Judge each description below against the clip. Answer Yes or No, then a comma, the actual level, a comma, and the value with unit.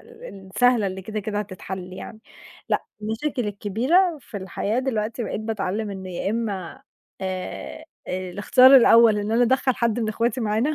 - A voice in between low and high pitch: No, high, 215 Hz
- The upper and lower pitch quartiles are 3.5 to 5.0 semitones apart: Yes, average, 3.8 semitones